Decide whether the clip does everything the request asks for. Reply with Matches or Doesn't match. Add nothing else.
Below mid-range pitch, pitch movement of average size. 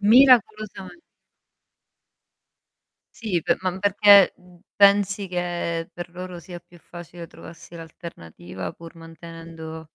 Doesn't match